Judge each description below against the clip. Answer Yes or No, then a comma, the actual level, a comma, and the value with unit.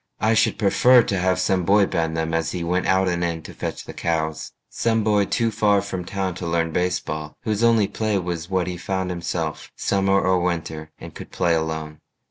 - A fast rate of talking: Yes, fast, 210 wpm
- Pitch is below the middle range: Yes, very low, 90 Hz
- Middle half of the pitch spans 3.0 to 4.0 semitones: Yes, average, 3.3 semitones